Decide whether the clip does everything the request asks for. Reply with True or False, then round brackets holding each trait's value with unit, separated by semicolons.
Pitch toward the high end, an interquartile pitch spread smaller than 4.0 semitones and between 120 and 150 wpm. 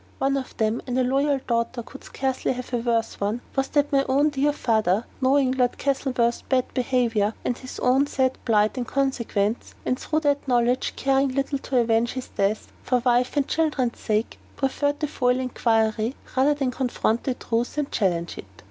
False (255 Hz; 2.7 semitones; 185 wpm)